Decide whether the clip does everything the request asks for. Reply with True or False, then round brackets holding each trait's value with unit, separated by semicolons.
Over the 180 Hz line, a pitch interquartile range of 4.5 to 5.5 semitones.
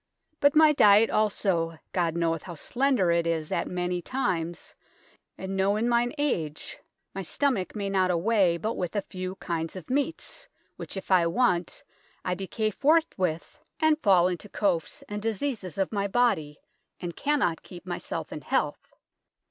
True (190 Hz; 5.1 semitones)